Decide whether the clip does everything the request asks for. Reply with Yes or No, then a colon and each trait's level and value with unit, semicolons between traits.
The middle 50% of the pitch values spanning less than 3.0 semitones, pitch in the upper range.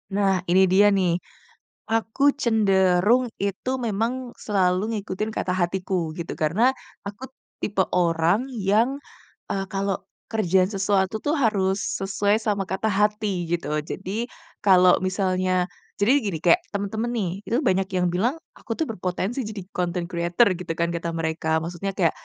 Yes: narrow, 2.6 semitones; high, 195 Hz